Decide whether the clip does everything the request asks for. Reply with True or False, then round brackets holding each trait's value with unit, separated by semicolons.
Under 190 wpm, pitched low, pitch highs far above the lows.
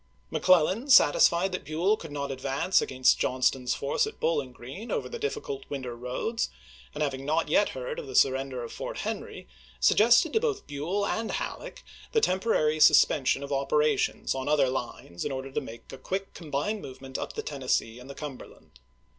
False (180 wpm; 145 Hz; 7.2 semitones)